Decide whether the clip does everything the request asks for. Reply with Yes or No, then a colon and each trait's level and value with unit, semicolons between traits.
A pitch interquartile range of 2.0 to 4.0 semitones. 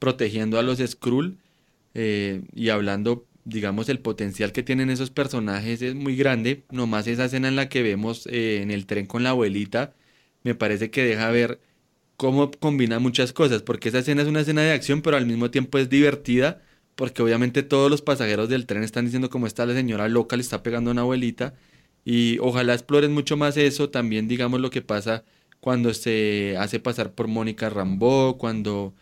Yes: average, 3.0 semitones